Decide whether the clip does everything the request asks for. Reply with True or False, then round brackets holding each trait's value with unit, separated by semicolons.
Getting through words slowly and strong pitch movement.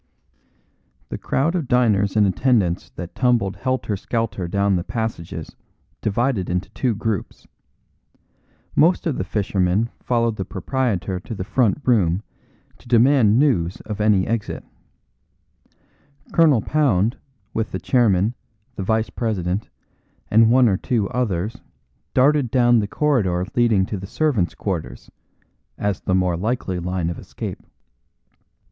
False (130 wpm; 4.8 semitones)